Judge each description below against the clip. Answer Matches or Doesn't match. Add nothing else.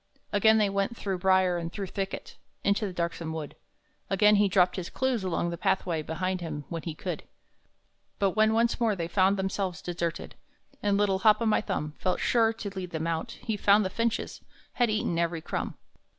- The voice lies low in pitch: Doesn't match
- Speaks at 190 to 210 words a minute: Matches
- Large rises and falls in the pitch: Doesn't match